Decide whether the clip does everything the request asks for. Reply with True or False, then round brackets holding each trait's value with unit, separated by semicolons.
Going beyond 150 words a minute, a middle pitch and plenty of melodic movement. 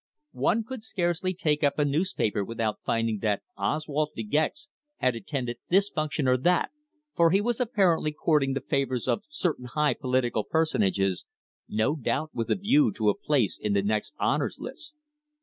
True (170 wpm; 150 Hz; 7.5 semitones)